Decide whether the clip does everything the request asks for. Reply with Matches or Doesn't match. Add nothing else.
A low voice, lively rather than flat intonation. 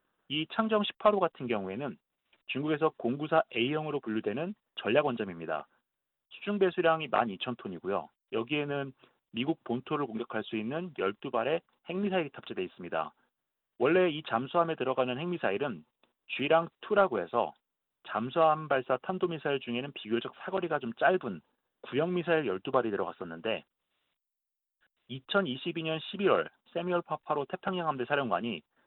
Doesn't match